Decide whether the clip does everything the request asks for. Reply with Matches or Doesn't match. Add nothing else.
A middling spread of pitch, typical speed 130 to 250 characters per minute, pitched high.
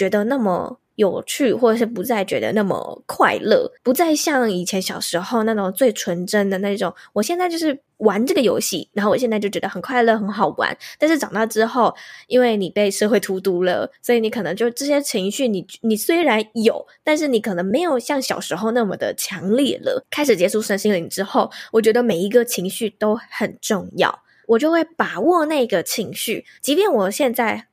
Doesn't match